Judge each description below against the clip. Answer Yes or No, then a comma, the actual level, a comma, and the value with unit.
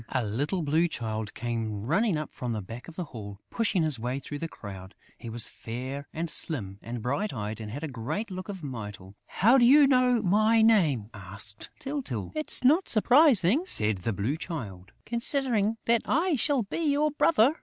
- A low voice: No, medium, 155 Hz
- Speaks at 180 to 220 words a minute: Yes, average, 190 wpm